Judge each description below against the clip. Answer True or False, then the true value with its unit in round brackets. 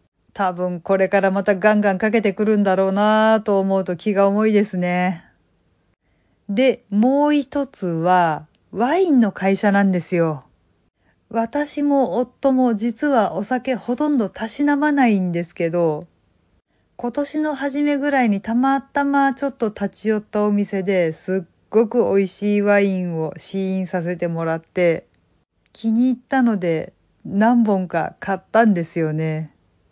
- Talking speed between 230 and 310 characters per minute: True (275 characters per minute)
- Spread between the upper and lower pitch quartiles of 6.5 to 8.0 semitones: False (5.3 semitones)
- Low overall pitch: False (200 Hz)